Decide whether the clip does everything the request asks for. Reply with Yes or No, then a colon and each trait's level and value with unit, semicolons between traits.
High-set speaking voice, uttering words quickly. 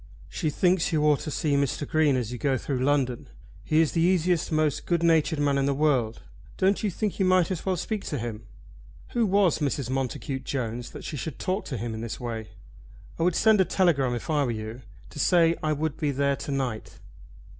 No: medium, 145 Hz; fast, 220 wpm